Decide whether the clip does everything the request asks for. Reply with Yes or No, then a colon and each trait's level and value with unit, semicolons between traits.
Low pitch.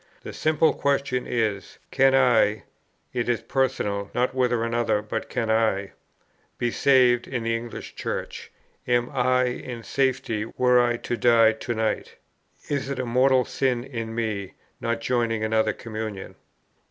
Yes: low, 120 Hz